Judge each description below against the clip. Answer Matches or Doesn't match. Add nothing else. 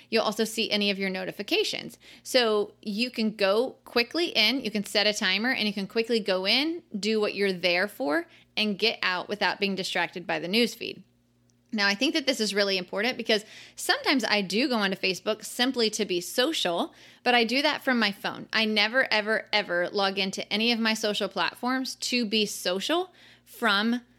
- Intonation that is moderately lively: Matches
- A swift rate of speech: Doesn't match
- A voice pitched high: Matches